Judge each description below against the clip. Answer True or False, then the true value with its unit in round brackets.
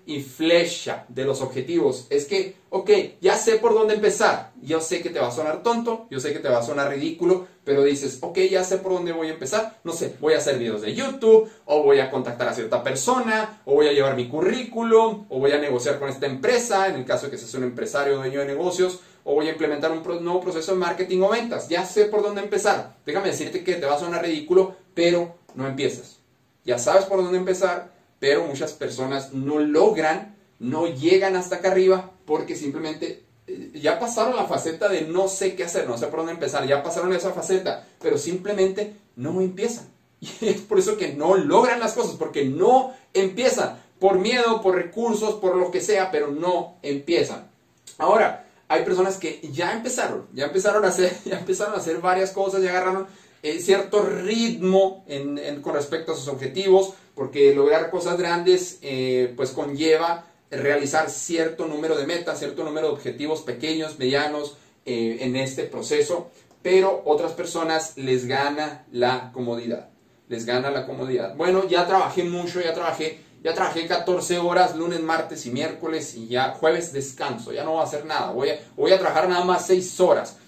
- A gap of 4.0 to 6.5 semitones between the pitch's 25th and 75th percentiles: True (4.5 semitones)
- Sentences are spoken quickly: True (195 wpm)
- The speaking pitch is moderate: True (175 Hz)